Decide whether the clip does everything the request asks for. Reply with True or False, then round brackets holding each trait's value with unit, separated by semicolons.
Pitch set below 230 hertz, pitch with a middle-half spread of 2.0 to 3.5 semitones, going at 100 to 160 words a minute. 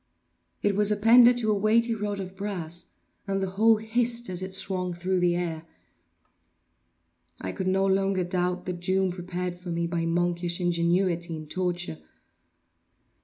True (185 Hz; 2.4 semitones; 155 wpm)